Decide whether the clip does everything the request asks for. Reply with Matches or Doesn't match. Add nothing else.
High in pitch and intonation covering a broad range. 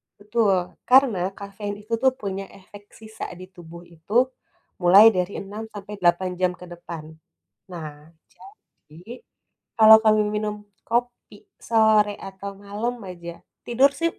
Doesn't match